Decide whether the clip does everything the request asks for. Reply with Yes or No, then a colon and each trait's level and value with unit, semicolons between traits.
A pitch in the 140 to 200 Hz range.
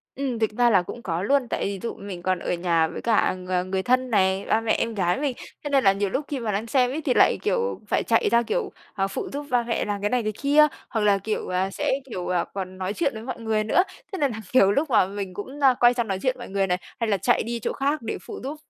No: high, 220 Hz